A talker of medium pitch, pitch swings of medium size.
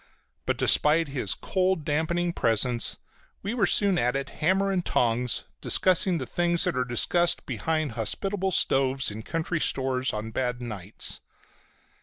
No: medium, 150 Hz; wide, 6.0 semitones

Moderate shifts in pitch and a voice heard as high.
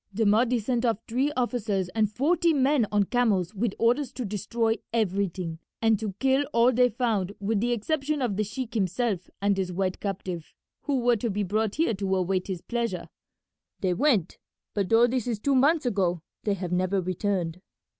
Yes: average, 4.2 semitones; high, 215 Hz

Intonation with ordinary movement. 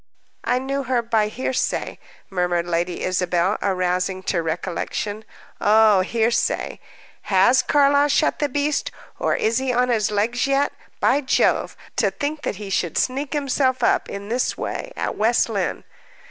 No: wide, 5.7 semitones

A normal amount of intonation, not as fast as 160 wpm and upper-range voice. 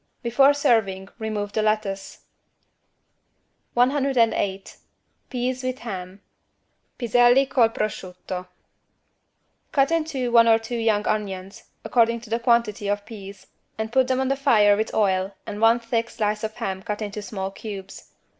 Yes: average, 3.0 semitones; average, 145 wpm; high, 220 Hz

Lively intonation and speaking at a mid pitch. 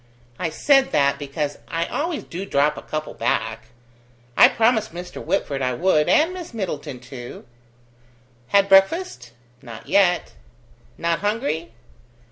Yes: wide, 6.7 semitones; medium, 170 Hz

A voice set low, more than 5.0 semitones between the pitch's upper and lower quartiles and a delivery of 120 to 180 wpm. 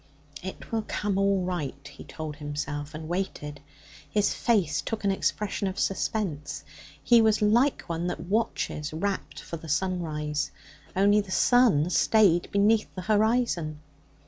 No: medium, 185 Hz; wide, 5.5 semitones; average, 145 wpm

